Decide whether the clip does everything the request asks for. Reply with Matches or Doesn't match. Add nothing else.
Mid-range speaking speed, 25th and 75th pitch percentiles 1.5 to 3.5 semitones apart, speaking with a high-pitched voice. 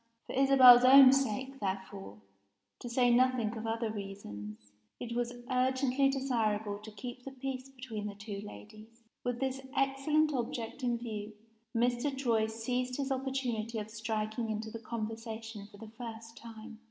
Matches